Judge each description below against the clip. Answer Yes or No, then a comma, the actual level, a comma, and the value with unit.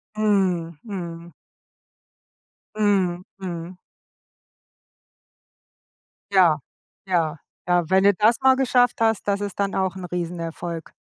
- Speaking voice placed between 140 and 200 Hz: Yes, medium, 185 Hz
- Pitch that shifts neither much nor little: Yes, average, 3.1 semitones